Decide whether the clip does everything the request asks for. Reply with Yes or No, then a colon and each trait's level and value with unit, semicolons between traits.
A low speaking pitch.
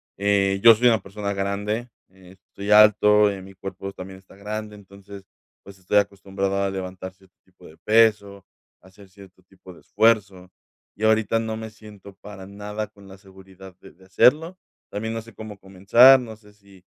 Yes: low, 100 Hz